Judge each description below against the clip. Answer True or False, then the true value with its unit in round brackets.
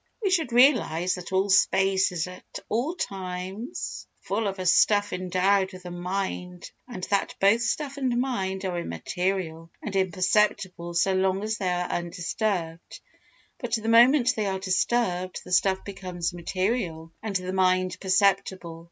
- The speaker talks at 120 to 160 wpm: True (150 wpm)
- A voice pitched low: False (190 Hz)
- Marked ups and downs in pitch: False (2.7 semitones)